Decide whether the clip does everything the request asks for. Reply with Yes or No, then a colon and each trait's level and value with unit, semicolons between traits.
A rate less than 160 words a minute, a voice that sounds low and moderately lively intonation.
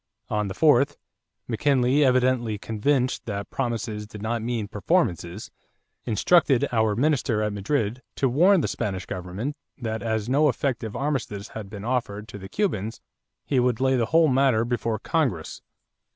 Yes: average, 150 wpm; low, 120 Hz; average, 4.2 semitones